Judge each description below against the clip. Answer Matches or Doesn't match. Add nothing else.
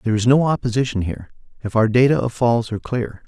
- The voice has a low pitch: Matches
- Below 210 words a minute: Doesn't match